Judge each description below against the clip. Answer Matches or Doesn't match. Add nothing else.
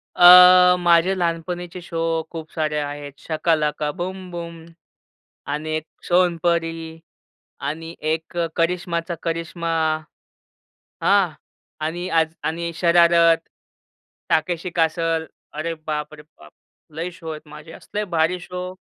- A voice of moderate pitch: Matches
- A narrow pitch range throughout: Matches